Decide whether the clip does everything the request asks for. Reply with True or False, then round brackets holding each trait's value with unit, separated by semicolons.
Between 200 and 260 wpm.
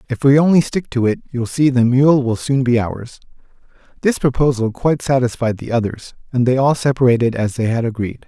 True (205 wpm)